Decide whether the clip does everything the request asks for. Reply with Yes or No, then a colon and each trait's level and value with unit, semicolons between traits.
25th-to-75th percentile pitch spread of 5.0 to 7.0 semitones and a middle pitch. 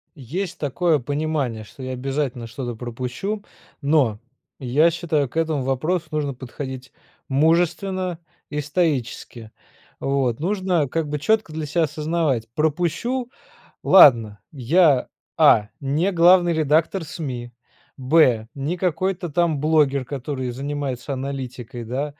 No: average, 4.4 semitones; medium, 145 Hz